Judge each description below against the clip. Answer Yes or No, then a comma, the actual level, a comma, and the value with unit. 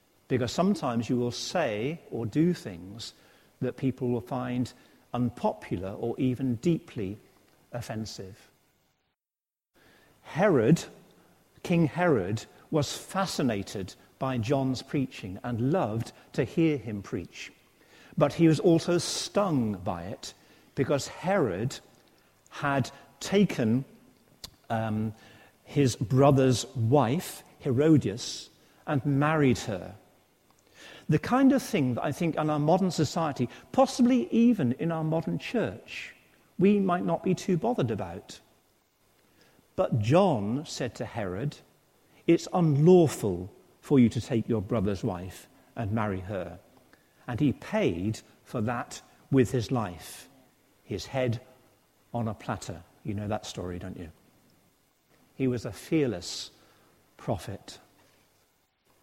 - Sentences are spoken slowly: Yes, slow, 115 wpm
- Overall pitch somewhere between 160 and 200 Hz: No, low, 130 Hz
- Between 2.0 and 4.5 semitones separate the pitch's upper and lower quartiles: No, wide, 5.6 semitones